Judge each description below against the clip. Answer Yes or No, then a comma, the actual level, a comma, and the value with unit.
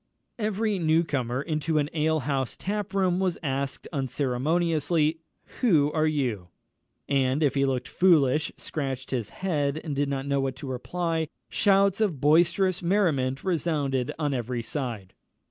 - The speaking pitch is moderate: Yes, medium, 150 Hz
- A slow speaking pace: No, average, 145 wpm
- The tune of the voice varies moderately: Yes, average, 4.2 semitones